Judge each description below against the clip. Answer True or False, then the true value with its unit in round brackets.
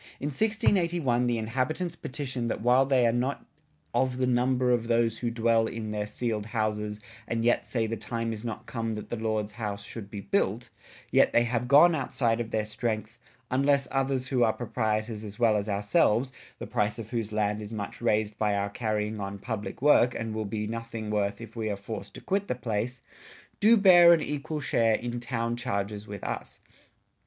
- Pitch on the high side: False (115 Hz)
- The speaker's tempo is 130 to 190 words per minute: False (200 wpm)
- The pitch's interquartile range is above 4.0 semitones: False (2.9 semitones)